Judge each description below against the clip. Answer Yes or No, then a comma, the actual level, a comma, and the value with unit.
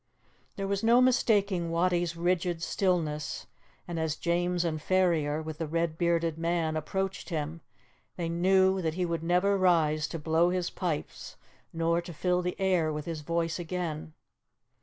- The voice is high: No, medium, 170 Hz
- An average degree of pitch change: No, narrow, 2.2 semitones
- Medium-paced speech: Yes, average, 160 wpm